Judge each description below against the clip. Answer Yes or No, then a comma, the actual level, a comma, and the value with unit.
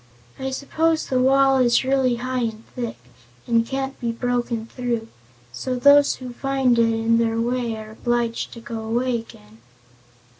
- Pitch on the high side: Yes, high, 240 Hz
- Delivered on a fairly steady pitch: Yes, narrow, 2.3 semitones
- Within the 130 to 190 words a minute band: Yes, average, 160 wpm